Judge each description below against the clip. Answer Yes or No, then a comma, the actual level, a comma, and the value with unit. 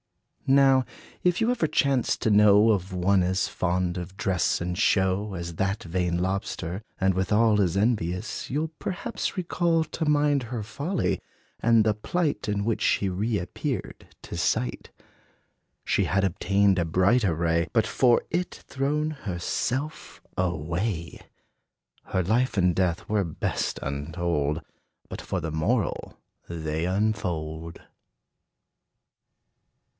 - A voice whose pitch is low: Yes, low, 100 Hz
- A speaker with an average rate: No, slow, 130 wpm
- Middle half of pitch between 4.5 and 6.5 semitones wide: Yes, wide, 5.5 semitones